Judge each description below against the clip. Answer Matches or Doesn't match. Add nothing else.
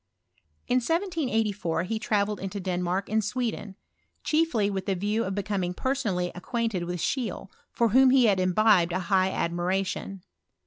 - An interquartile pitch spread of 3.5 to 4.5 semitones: Matches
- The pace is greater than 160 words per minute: Doesn't match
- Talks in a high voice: Matches